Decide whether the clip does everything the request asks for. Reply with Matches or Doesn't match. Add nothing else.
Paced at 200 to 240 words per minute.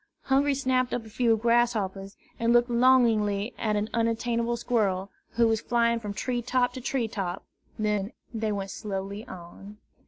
Doesn't match